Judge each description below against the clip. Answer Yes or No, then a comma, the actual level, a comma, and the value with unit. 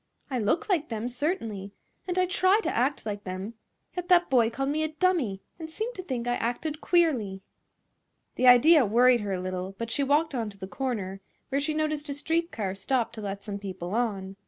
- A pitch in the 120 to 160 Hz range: No, high, 245 Hz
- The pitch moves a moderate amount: No, wide, 7.4 semitones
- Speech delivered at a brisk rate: Yes, fast, 210 wpm